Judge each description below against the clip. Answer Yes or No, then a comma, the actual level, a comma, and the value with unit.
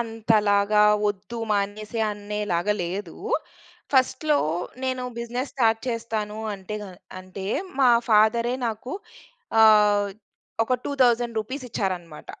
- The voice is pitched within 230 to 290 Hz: No, high, 215 Hz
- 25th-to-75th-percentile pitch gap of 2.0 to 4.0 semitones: Yes, narrow, 2.5 semitones